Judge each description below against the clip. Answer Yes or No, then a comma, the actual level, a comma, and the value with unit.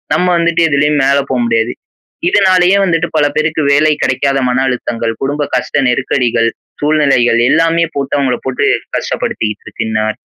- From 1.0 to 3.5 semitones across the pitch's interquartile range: No, average, 4.1 semitones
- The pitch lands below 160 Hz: Yes, medium, 140 Hz